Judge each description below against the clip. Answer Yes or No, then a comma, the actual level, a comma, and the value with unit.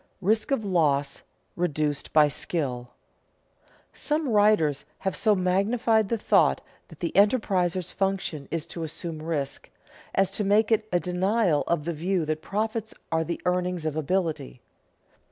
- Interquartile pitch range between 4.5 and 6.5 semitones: Yes, average, 4.8 semitones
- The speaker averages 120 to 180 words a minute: Yes, average, 150 wpm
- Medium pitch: Yes, medium, 180 Hz